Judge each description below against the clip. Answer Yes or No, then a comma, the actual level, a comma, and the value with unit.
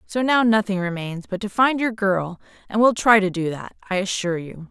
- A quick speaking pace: Yes, fast, 230 wpm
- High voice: Yes, high, 200 Hz